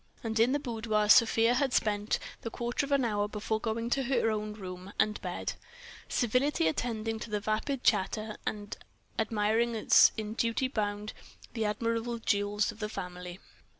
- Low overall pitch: No, high, 220 Hz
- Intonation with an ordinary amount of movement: No, narrow, 2.1 semitones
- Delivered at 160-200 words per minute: Yes, average, 165 wpm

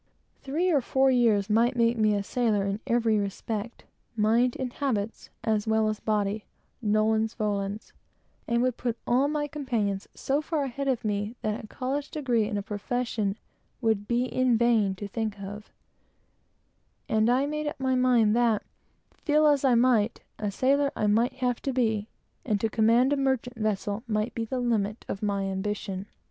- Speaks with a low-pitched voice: No, high, 225 Hz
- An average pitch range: Yes, average, 3.4 semitones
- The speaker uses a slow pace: No, average, 170 wpm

